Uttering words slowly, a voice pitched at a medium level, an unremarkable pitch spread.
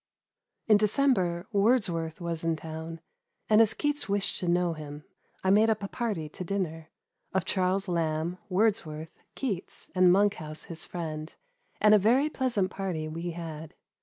No: average, 155 wpm; medium, 180 Hz; average, 4.2 semitones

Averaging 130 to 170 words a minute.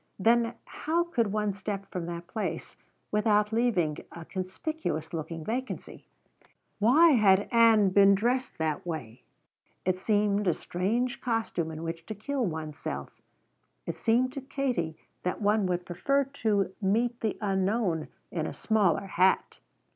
Yes: average, 145 wpm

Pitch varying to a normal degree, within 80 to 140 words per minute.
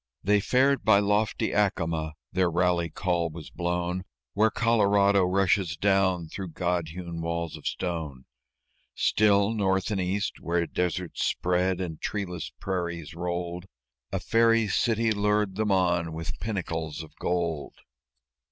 Yes: average, 3.1 semitones; slow, 135 wpm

